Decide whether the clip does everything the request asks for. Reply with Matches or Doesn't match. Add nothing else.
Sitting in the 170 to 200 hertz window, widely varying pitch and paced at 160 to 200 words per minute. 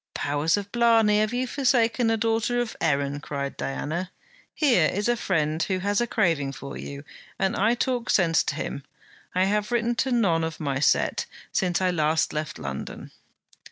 Matches